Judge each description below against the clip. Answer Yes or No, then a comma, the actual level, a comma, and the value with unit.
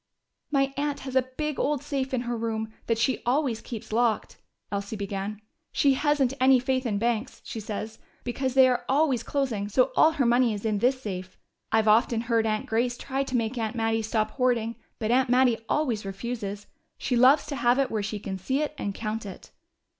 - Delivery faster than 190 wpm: Yes, fast, 205 wpm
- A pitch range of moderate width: Yes, average, 3.4 semitones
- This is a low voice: No, high, 240 Hz